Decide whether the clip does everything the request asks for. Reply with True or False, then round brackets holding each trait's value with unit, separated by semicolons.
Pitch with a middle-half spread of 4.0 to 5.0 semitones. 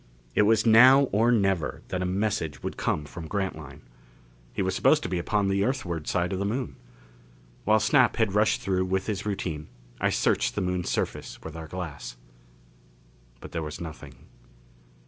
True (4.4 semitones)